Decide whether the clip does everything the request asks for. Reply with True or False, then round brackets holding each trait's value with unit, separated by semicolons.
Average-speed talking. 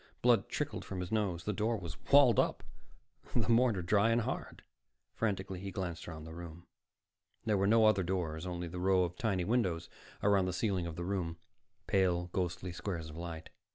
True (190 wpm)